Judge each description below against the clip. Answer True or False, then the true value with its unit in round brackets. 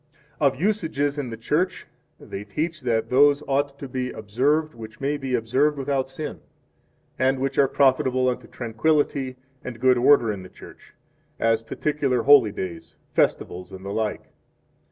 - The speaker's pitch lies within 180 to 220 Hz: False (130 Hz)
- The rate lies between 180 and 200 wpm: False (160 wpm)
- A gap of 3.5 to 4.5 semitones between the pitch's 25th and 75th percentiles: True (4.1 semitones)